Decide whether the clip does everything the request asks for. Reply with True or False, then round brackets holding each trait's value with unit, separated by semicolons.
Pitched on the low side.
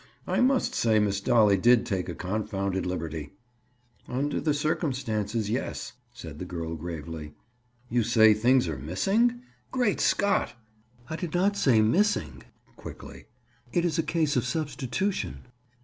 True (115 Hz)